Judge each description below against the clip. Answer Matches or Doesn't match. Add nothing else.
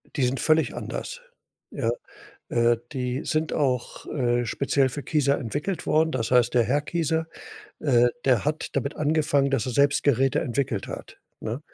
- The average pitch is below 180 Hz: Matches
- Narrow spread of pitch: Doesn't match